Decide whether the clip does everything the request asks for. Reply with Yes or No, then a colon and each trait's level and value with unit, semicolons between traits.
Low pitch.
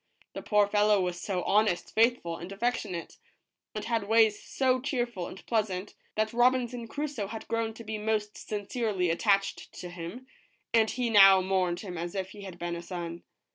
No: high, 210 Hz